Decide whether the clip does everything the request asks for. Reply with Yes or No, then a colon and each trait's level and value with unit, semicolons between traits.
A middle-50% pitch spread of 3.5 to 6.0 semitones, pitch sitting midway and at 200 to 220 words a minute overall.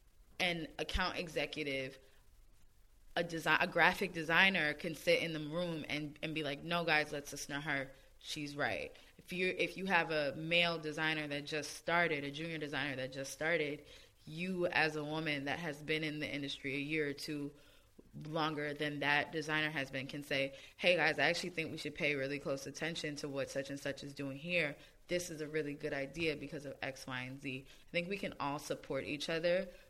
No: narrow, 2.6 semitones; medium, 150 Hz; fast, 205 wpm